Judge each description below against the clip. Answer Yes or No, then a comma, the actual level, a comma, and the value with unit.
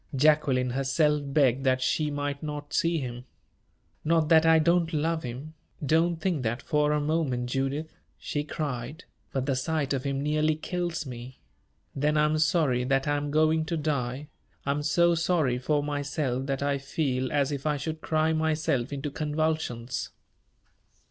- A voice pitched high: No, medium, 145 Hz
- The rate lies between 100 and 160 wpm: No, average, 170 wpm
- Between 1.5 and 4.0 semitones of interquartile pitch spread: Yes, average, 2.8 semitones